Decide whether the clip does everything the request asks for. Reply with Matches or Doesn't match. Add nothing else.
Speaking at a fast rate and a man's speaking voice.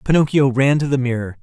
Matches